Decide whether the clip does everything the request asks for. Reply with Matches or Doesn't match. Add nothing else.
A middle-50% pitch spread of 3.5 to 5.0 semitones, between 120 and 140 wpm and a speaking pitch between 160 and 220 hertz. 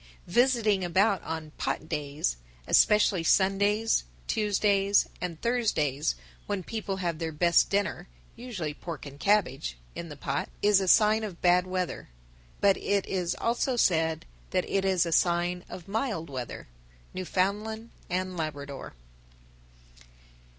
Matches